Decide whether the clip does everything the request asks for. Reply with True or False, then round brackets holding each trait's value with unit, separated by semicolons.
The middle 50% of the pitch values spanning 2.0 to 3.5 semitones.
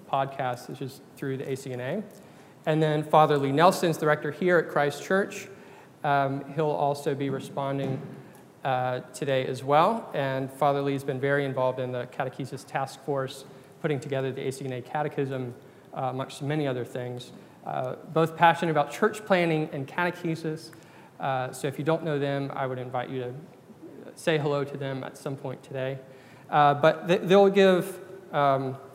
True (3.1 semitones)